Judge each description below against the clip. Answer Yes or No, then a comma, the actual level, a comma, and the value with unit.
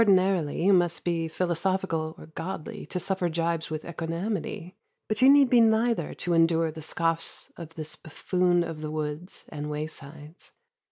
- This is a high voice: No, medium, 165 Hz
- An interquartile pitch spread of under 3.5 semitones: Yes, average, 2.8 semitones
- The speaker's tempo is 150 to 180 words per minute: Yes, average, 160 wpm